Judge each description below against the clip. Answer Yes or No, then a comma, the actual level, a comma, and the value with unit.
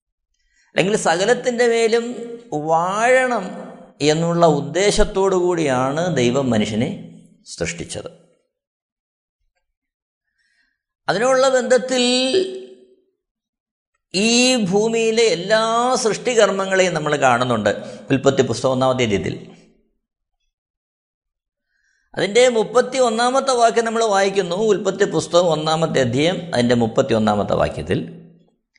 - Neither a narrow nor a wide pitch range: No, wide, 8.0 semitones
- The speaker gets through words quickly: No, average, 75 wpm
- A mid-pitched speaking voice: No, high, 200 Hz